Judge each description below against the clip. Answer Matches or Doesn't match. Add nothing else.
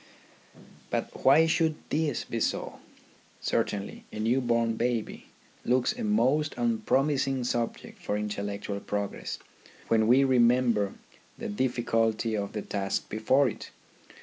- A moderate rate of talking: Doesn't match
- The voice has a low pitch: Matches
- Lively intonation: Doesn't match